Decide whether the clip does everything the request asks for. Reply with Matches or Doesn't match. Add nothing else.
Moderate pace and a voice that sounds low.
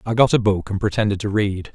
Doesn't match